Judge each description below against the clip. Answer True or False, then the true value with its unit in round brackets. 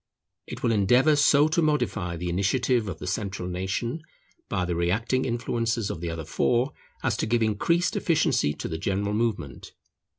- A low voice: True (110 Hz)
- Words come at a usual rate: True (170 wpm)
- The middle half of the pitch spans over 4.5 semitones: True (5.5 semitones)